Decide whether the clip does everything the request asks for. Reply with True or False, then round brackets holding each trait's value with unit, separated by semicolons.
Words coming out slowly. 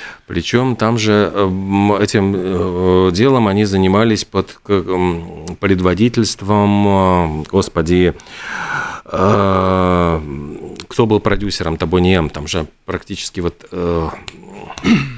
True (70 wpm)